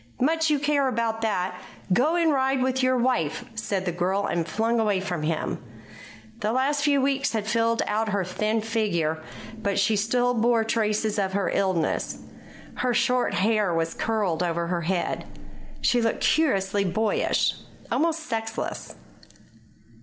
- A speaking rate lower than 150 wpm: No, average, 155 wpm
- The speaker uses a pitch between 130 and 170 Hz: No, high, 220 Hz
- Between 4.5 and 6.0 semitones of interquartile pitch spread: Yes, average, 4.8 semitones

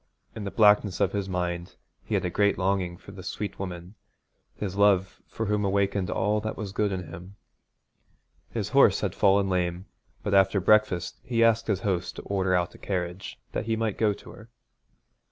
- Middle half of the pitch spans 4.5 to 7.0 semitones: No, narrow, 2.4 semitones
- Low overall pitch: Yes, low, 100 Hz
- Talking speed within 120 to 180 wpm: No, average, 190 wpm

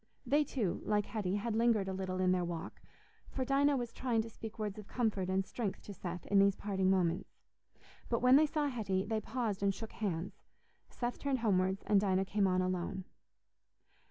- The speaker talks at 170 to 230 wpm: Yes, average, 195 wpm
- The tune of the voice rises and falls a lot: No, average, 3.8 semitones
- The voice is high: Yes, high, 205 Hz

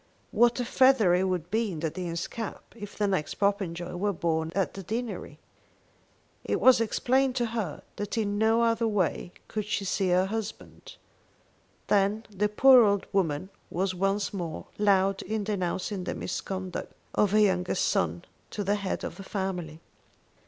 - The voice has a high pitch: Yes, high, 200 Hz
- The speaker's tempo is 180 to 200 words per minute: No, average, 165 wpm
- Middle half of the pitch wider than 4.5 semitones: No, average, 3.0 semitones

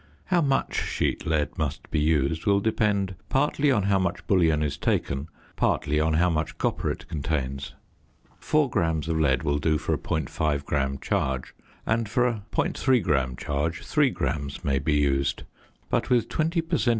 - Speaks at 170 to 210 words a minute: Yes, average, 175 wpm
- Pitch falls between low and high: No, very low, 80 Hz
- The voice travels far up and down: Yes, wide, 6.8 semitones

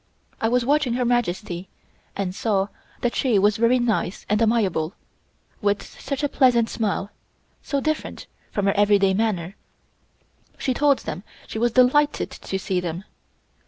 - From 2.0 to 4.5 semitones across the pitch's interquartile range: Yes, average, 4.1 semitones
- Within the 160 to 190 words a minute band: No, average, 150 wpm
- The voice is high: Yes, high, 220 Hz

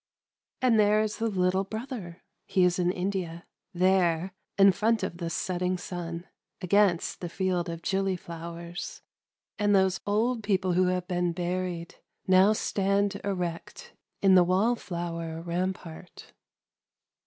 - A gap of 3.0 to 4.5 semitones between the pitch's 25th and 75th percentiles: No, narrow, 2.4 semitones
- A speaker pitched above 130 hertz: Yes, medium, 185 Hz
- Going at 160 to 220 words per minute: No, average, 150 wpm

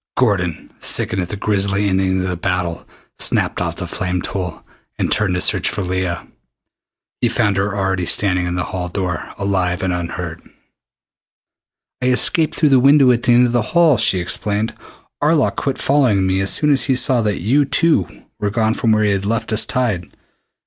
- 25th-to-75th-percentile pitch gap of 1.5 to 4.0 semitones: No, average, 5.0 semitones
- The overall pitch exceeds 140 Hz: No, low, 100 Hz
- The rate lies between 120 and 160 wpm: No, average, 190 wpm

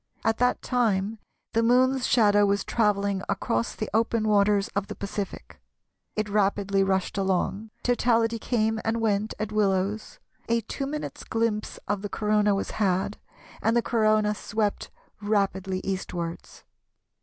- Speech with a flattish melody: Yes, narrow, 2.2 semitones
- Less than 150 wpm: Yes, average, 140 wpm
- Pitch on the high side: Yes, high, 210 Hz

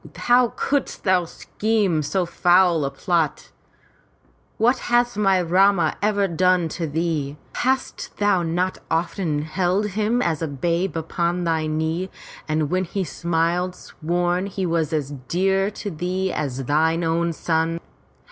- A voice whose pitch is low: No, medium, 175 Hz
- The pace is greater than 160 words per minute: No, average, 140 wpm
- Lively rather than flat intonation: No, average, 3.0 semitones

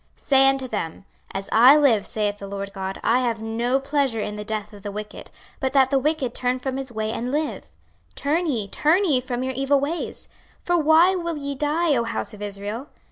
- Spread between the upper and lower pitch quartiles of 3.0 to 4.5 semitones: No, average, 4.9 semitones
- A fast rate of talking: Yes, fast, 220 wpm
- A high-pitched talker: Yes, very high, 255 Hz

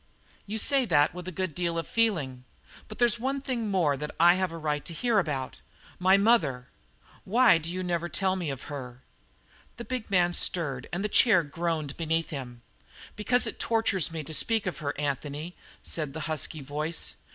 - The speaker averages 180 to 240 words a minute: Yes, average, 190 wpm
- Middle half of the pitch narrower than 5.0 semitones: No, average, 5.3 semitones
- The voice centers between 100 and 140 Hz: No, medium, 170 Hz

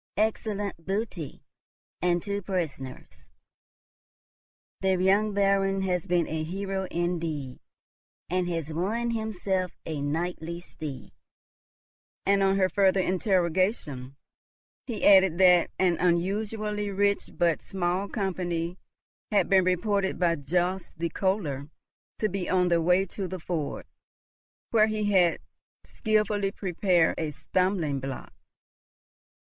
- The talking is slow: Yes, slow, 115 wpm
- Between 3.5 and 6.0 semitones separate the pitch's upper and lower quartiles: No, average, 2.7 semitones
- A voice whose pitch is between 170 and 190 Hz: Yes, medium, 185 Hz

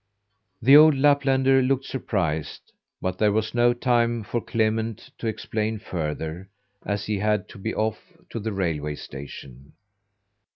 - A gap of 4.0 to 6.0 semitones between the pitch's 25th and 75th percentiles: Yes, average, 4.5 semitones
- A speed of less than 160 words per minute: Yes, average, 140 wpm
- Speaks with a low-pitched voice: Yes, low, 110 Hz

